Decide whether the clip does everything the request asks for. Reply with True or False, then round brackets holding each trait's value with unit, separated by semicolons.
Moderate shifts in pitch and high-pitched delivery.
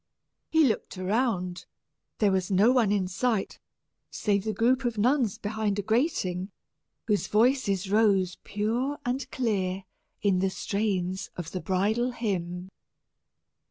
True (3.9 semitones; 205 Hz)